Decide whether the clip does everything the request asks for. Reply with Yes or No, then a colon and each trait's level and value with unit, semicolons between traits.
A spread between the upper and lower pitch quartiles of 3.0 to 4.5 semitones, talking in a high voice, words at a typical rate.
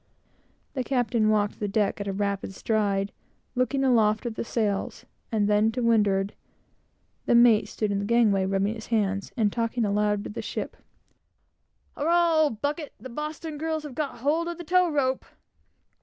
No: average, 5.2 semitones; high, 225 Hz; average, 170 wpm